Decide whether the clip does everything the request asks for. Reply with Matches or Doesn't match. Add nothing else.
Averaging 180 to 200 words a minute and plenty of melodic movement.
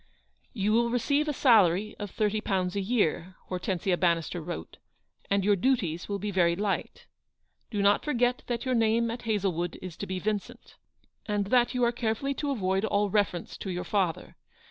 Doesn't match